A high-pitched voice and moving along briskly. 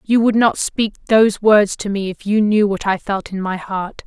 Yes: high, 205 Hz; fast, 250 wpm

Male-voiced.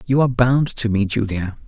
Yes: male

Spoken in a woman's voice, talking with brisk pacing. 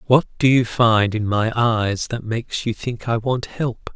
No: male; fast, 210 wpm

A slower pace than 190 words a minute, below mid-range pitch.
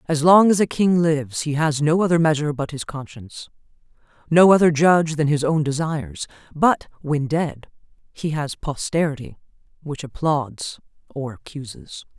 No: average, 150 wpm; medium, 150 Hz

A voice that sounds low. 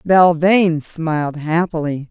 No: medium, 165 Hz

